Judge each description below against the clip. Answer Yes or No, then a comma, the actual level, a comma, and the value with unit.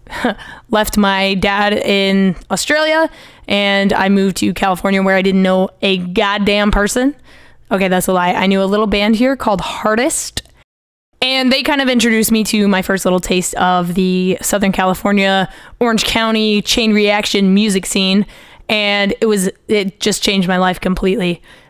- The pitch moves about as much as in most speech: No, narrow, 2.1 semitones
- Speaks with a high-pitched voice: Yes, high, 200 Hz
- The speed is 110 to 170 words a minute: Yes, average, 165 wpm